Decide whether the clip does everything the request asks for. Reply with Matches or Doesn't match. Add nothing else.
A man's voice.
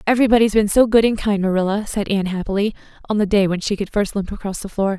Doesn't match